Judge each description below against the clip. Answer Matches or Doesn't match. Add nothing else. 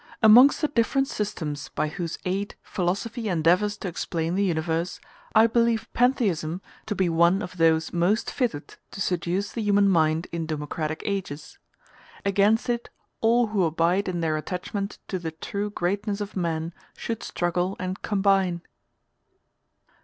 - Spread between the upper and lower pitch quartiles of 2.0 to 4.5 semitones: Matches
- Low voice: Doesn't match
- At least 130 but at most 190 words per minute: Matches